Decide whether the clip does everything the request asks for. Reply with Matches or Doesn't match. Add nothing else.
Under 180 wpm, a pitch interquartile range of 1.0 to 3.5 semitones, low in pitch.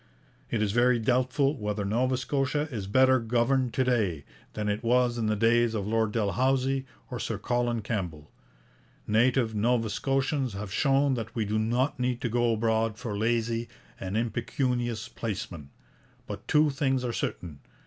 Matches